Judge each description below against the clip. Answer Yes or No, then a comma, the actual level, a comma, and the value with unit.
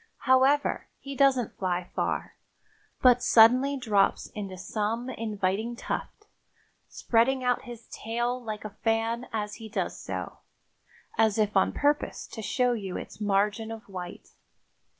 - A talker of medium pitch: No, high, 225 Hz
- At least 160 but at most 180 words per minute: No, slow, 135 wpm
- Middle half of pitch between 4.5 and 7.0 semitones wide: No, average, 3.1 semitones